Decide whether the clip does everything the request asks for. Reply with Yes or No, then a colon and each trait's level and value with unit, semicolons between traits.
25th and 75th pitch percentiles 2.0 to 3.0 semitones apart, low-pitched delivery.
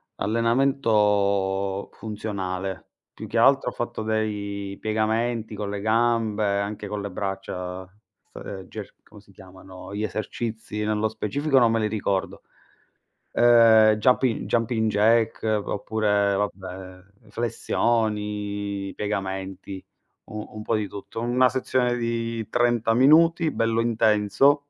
Yes: narrow, 2.5 semitones; low, 110 Hz